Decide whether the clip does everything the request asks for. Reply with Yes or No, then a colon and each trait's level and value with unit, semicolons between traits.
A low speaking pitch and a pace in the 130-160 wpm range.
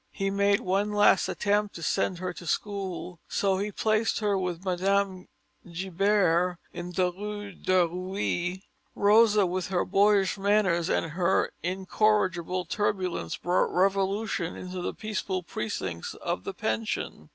No: high, 190 Hz; average, 140 wpm